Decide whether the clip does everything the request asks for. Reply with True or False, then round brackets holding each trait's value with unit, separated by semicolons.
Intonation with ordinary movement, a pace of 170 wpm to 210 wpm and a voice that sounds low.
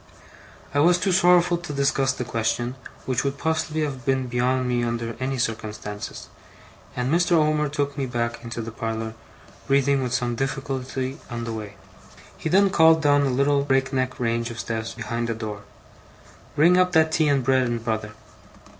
True (3.7 semitones; 180 wpm; 130 Hz)